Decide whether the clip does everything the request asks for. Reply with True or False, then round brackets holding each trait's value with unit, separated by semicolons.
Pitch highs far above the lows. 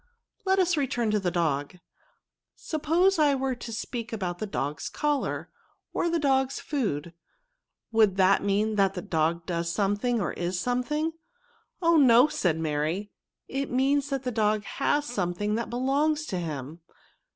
True (7.7 semitones)